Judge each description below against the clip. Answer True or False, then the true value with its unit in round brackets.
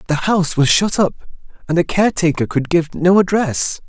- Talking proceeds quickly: False (185 wpm)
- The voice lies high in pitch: False (170 Hz)